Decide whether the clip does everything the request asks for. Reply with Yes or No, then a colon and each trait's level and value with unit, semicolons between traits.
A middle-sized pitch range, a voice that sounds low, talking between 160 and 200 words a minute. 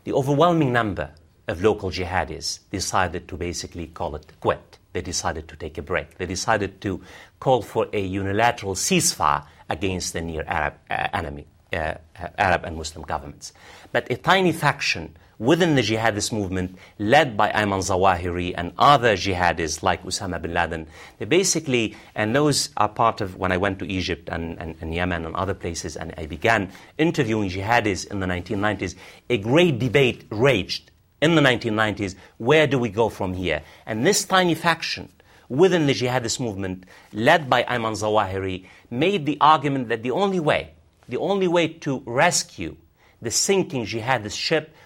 No: wide, 6.3 semitones; low, 100 Hz; average, 165 wpm